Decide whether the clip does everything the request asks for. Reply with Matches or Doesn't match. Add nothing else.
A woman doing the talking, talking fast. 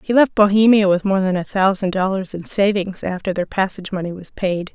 Matches